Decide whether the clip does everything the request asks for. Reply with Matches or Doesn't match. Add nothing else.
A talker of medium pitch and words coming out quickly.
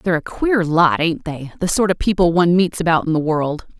Matches